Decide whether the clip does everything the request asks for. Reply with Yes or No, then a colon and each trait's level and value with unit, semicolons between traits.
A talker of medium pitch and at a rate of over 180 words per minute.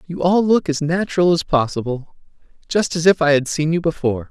Yes: medium, 160 Hz; average, 195 wpm